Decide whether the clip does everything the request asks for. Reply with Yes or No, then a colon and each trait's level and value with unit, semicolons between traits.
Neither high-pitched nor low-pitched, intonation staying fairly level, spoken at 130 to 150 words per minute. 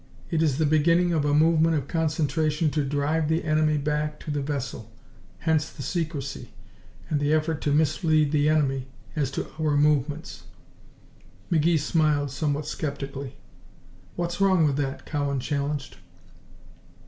Yes: medium, 150 Hz; narrow, 1.8 semitones; average, 145 wpm